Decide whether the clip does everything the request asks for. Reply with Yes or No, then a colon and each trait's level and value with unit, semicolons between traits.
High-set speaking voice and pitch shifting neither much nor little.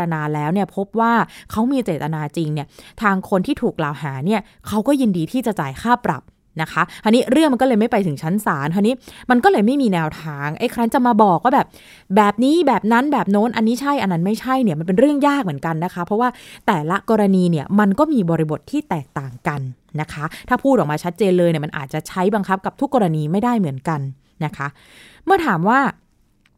No: high, 200 Hz; wide, 6.9 semitones